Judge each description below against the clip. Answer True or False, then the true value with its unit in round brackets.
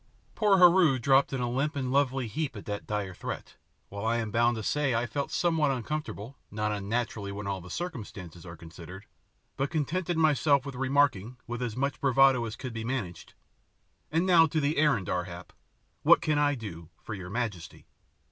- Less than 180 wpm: False (190 wpm)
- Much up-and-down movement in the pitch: True (5.8 semitones)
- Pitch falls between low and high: False (125 Hz)